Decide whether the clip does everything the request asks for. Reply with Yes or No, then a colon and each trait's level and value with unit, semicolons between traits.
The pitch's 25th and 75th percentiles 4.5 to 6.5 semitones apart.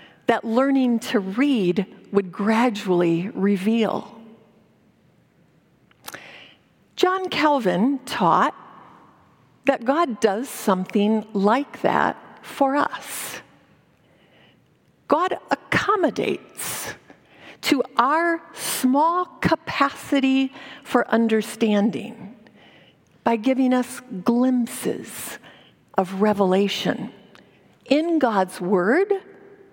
Yes: average, 4.9 semitones